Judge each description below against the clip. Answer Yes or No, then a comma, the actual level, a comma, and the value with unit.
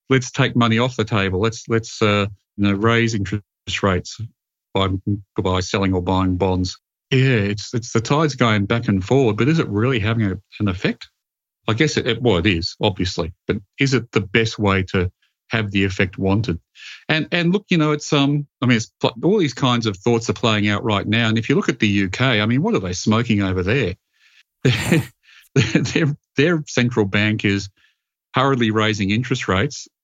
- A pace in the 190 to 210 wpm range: Yes, average, 200 wpm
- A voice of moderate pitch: No, low, 110 Hz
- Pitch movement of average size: Yes, average, 3.9 semitones